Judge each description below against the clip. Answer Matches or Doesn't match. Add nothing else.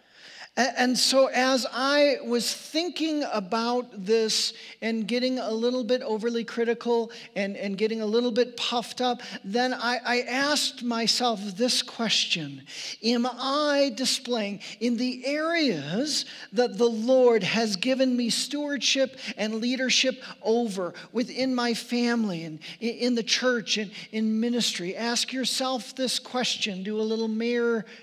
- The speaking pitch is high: Matches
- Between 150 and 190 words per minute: Doesn't match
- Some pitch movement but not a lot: Doesn't match